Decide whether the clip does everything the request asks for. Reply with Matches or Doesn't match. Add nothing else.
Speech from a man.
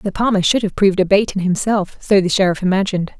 Doesn't match